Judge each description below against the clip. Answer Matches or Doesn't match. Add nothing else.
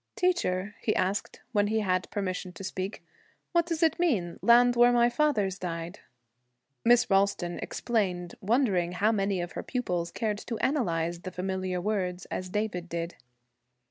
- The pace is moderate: Matches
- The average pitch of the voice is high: Matches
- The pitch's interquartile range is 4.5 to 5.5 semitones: Matches